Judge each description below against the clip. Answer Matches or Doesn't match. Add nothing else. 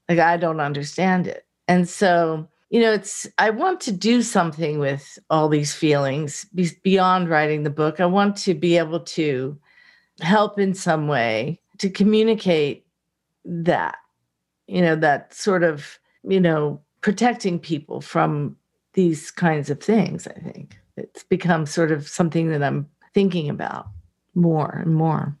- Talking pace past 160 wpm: Doesn't match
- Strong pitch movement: Doesn't match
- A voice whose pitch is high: Doesn't match